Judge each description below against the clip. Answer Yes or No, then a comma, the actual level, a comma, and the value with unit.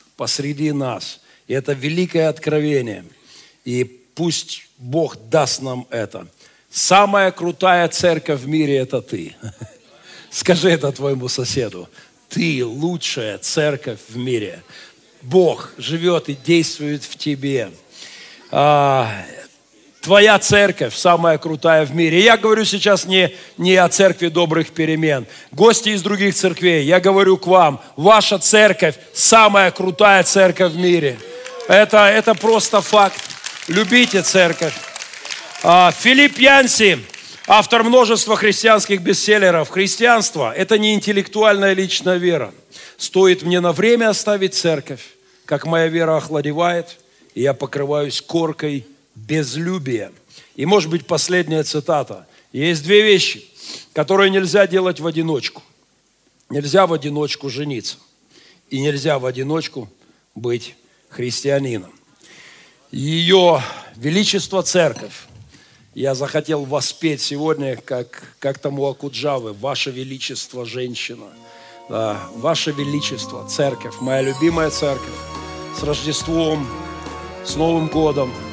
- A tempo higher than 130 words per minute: No, slow, 110 wpm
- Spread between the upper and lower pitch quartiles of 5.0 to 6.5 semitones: Yes, wide, 5.4 semitones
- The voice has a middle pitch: Yes, medium, 160 Hz